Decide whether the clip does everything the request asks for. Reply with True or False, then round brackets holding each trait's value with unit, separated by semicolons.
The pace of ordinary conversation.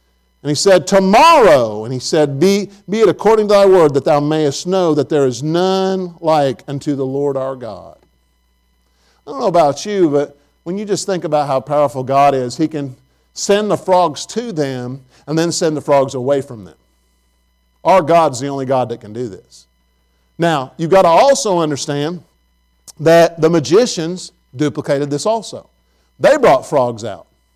True (180 wpm)